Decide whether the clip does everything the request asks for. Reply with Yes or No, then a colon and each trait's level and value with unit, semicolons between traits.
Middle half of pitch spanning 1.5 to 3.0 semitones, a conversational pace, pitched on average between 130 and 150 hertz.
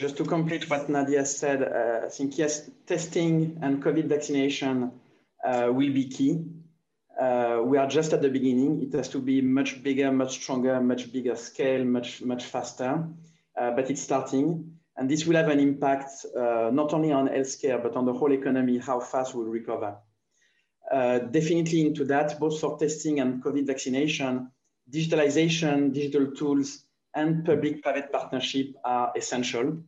Yes: average, 2.7 semitones; average, 165 wpm; medium, 140 Hz